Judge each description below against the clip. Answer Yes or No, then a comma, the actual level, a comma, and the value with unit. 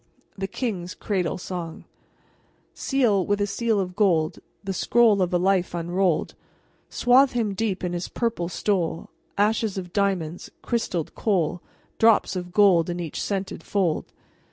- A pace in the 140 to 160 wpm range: Yes, average, 145 wpm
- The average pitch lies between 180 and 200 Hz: Yes, high, 190 Hz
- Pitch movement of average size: Yes, average, 3.1 semitones